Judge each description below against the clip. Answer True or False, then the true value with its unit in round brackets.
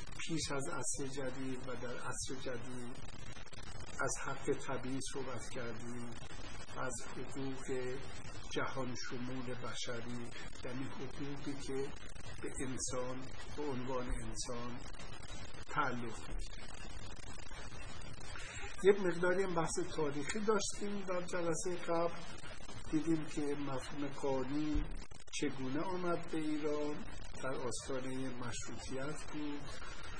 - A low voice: True (130 Hz)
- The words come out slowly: True (95 wpm)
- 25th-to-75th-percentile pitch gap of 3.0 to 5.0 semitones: True (3.5 semitones)